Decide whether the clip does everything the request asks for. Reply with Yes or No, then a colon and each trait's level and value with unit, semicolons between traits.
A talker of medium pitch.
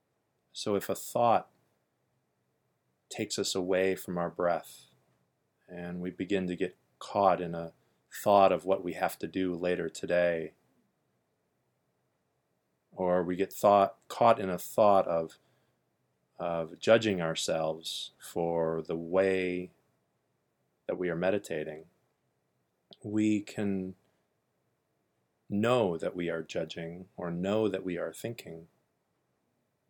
No: very low, 90 Hz